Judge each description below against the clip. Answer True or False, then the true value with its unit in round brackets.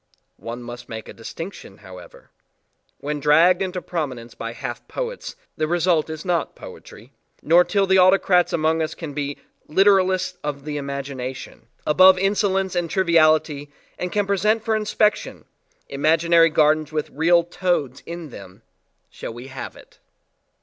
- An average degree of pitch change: True (4.6 semitones)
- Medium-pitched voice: True (160 Hz)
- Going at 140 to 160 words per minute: True (145 wpm)